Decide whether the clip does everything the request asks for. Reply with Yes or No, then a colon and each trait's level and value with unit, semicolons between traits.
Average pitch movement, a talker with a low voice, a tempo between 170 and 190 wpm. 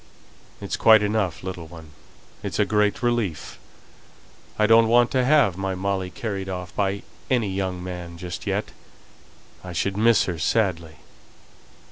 No: average, 3.5 semitones; very low, 95 Hz; average, 145 wpm